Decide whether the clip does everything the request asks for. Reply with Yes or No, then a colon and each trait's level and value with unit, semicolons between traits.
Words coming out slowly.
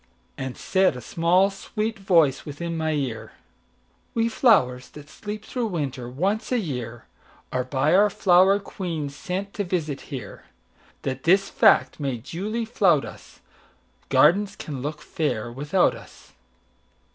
Yes: slow, 125 wpm